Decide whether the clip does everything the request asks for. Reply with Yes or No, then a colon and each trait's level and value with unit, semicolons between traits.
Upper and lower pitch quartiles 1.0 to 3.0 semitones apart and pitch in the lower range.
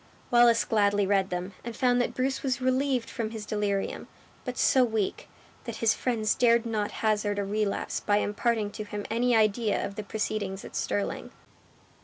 No: narrow, 2.6 semitones; high, 215 Hz